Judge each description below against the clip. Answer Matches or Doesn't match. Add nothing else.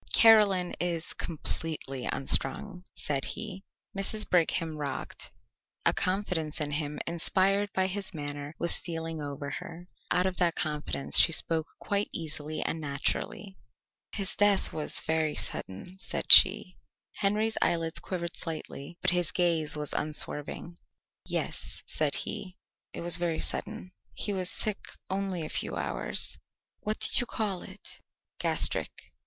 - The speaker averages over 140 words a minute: Doesn't match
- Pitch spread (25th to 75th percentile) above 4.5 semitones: Doesn't match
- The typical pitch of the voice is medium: Matches